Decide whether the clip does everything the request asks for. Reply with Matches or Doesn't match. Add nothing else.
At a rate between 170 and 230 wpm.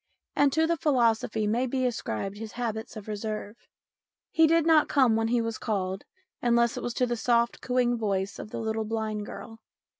Matches